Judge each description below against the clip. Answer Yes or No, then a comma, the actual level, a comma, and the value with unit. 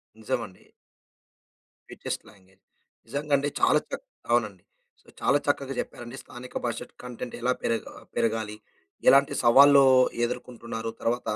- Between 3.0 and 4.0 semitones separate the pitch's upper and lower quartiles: Yes, average, 3.3 semitones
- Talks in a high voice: No, low, 120 Hz